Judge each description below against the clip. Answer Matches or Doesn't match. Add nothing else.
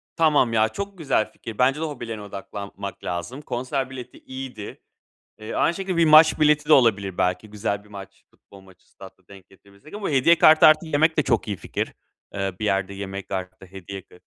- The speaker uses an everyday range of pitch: Doesn't match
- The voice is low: Matches